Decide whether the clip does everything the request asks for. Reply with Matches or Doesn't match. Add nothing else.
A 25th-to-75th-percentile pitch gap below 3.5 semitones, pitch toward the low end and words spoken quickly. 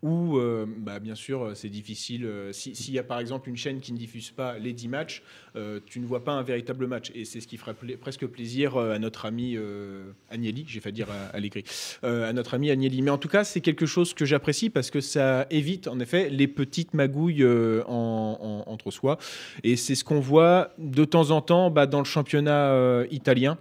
Doesn't match